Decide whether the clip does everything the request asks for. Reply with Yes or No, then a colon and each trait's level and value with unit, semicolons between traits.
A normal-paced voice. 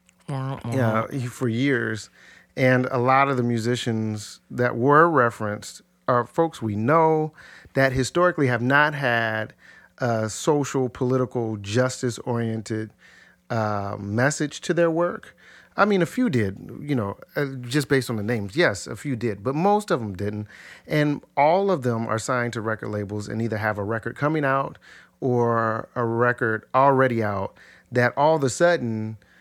Yes: average, 160 wpm